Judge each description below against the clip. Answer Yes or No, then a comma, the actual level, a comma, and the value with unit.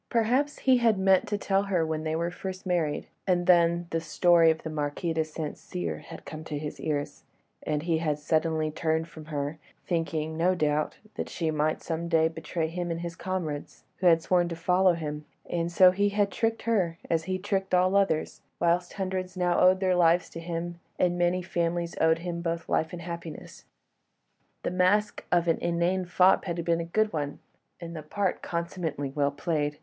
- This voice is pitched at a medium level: Yes, medium, 170 Hz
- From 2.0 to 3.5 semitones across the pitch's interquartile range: Yes, narrow, 2.4 semitones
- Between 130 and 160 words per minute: No, average, 195 wpm